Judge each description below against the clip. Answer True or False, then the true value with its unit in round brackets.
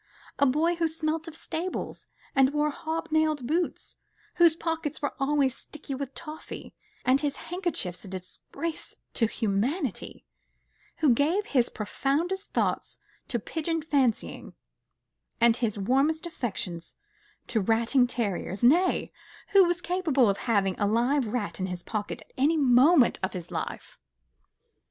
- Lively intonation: True (5.8 semitones)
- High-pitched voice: True (280 Hz)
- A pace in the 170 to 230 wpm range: False (140 wpm)